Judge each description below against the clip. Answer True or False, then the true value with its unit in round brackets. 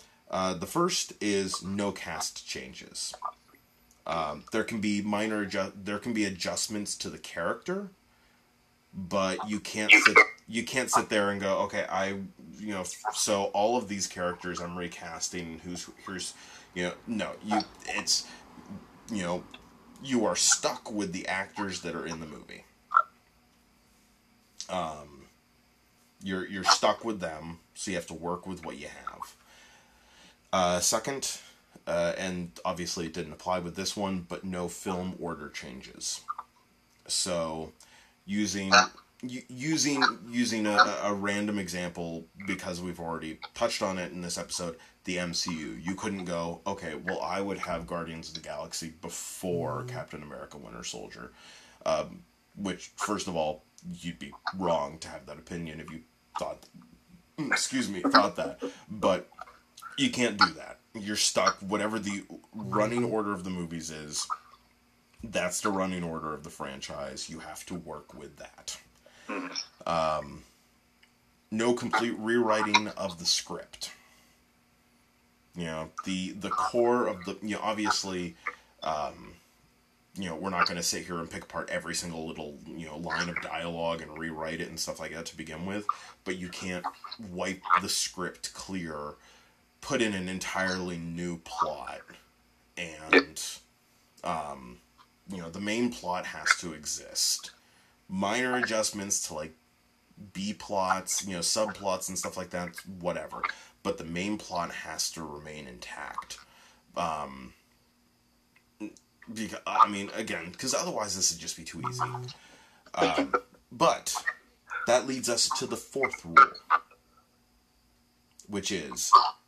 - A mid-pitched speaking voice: False (95 Hz)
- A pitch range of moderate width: True (3.8 semitones)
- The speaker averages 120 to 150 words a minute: True (145 wpm)